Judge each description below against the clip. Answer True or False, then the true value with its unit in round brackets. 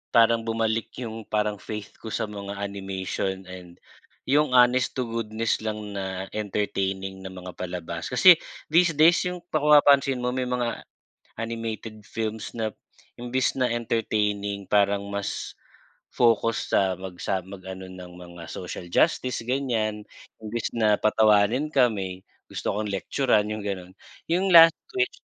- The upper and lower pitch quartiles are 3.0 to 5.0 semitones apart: True (3.8 semitones)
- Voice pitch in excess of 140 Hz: False (110 Hz)